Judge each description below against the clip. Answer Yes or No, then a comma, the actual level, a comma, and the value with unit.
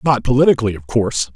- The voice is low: Yes, low, 115 Hz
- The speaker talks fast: No, average, 180 wpm